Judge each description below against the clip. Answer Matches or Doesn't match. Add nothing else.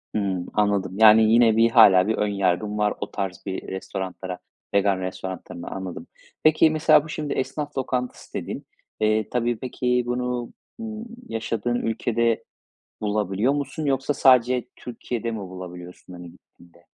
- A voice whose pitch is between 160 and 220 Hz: Doesn't match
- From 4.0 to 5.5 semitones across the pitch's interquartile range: Matches